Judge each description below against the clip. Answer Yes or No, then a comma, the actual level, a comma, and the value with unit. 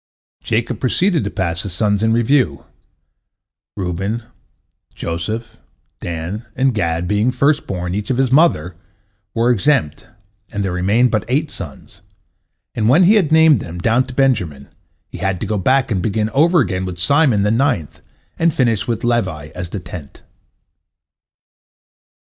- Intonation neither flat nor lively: No, wide, 6.2 semitones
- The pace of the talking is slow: No, average, 155 wpm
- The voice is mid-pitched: No, low, 110 Hz